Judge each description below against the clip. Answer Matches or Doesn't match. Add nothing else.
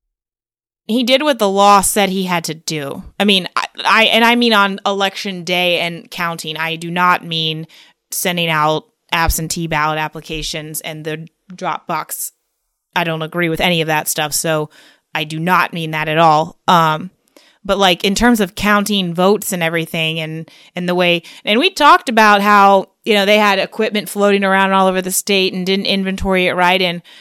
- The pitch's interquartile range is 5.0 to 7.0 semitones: Doesn't match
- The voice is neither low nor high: Matches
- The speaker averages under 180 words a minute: Doesn't match